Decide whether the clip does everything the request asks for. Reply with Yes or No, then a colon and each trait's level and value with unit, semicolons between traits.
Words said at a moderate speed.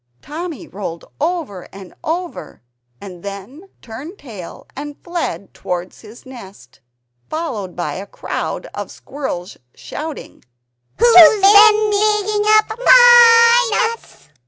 No: slow, 110 wpm